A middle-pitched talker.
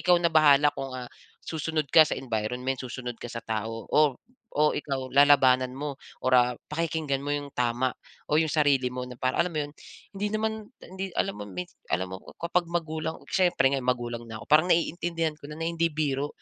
Yes: medium, 145 Hz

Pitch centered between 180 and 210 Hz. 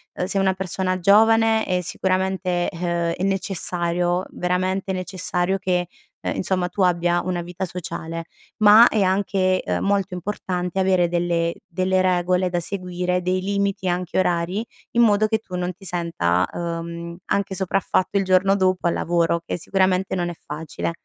Yes: medium, 185 Hz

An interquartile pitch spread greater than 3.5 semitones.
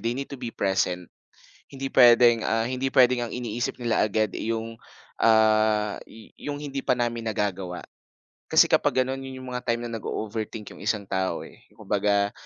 No: average, 2.8 semitones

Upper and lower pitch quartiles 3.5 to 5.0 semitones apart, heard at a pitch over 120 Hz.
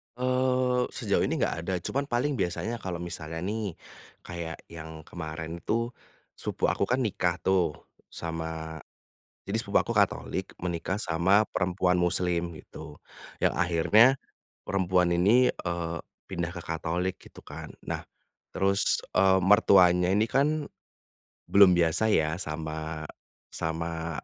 No: average, 3.8 semitones; very low, 90 Hz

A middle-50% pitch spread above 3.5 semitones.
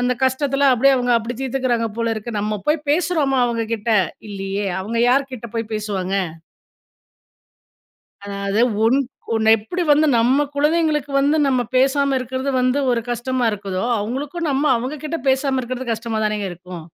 Yes: average, 4.0 semitones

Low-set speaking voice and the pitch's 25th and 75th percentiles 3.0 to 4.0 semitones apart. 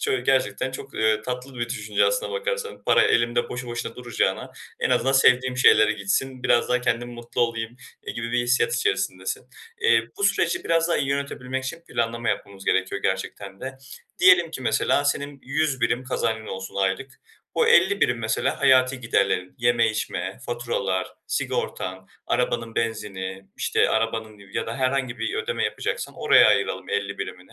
Yes: low, 125 Hz; average, 3.7 semitones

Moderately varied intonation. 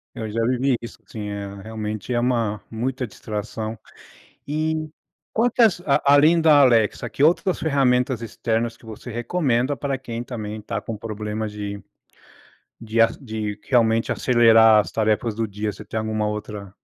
Yes: average, 3.4 semitones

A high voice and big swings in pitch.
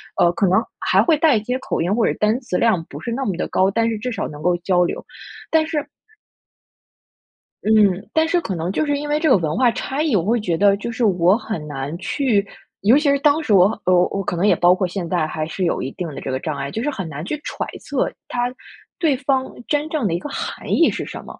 Yes: high, 210 Hz; wide, 7.0 semitones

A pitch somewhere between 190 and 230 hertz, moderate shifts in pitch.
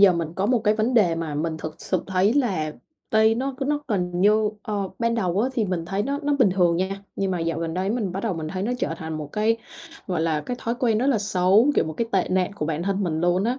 Yes: high, 195 Hz; average, 4.8 semitones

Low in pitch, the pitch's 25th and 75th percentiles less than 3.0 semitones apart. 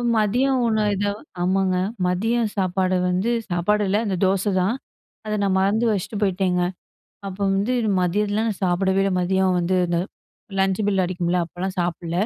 No: high, 190 Hz; narrow, 2.4 semitones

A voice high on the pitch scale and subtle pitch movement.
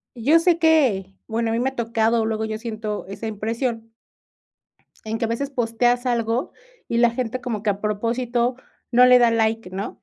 Yes: high, 230 Hz; narrow, 2.0 semitones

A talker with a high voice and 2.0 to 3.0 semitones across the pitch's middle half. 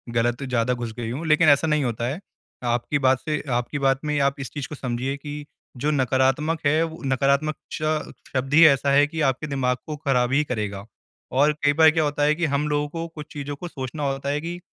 No: medium, 140 Hz; average, 2.7 semitones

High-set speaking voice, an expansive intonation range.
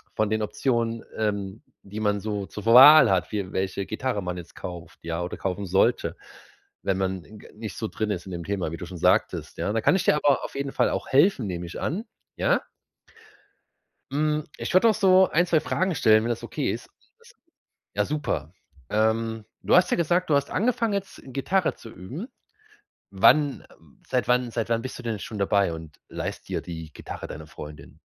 No: low, 110 Hz; wide, 7.1 semitones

